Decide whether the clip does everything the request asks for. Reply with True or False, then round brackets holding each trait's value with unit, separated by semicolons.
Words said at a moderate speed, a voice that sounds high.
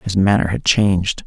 False (190 wpm; 95 Hz)